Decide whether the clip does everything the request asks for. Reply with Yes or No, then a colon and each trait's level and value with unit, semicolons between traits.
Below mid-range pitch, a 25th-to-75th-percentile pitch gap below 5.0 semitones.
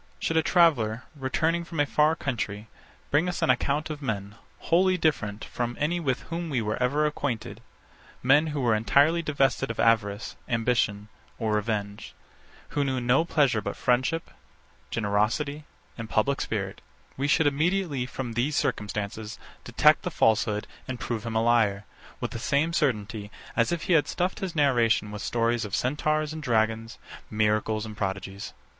No: low, 125 Hz; wide, 5.6 semitones